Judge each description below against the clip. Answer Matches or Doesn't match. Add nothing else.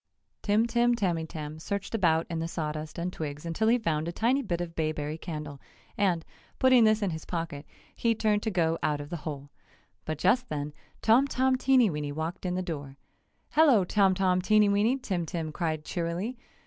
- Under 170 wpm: Doesn't match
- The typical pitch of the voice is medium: Matches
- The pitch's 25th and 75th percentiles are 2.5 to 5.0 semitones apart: Doesn't match